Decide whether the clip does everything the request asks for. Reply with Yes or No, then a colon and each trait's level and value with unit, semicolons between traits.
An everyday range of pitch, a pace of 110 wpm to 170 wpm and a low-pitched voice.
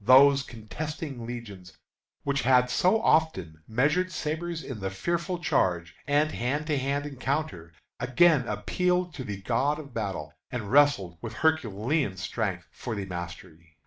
No: wide, 7.6 semitones; average, 145 wpm; low, 125 Hz